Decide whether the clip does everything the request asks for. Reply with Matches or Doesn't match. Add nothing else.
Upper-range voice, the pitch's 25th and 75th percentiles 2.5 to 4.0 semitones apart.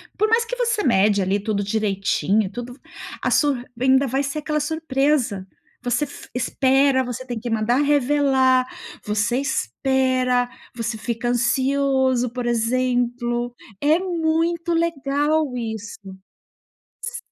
Matches